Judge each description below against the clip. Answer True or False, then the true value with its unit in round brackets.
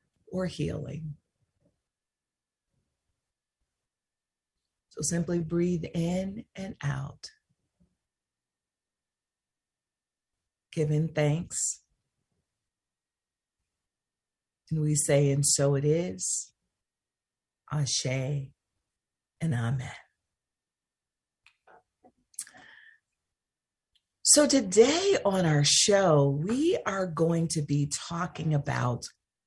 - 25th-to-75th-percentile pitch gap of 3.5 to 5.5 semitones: True (4.0 semitones)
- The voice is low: False (150 Hz)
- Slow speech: True (65 wpm)